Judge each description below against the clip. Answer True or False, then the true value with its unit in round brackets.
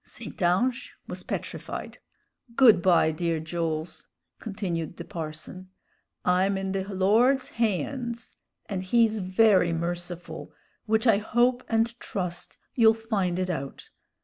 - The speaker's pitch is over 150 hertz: True (190 Hz)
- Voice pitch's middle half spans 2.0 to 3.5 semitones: False (4.4 semitones)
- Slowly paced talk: True (120 wpm)